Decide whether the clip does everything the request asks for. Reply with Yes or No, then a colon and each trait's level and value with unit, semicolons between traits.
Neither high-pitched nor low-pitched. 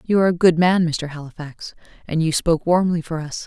Yes: medium, 165 Hz